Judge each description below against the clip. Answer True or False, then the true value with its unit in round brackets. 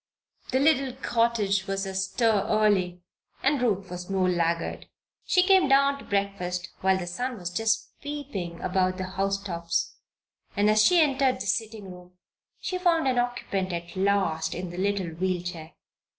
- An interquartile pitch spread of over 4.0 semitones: True (5.2 semitones)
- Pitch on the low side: False (195 Hz)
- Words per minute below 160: False (165 wpm)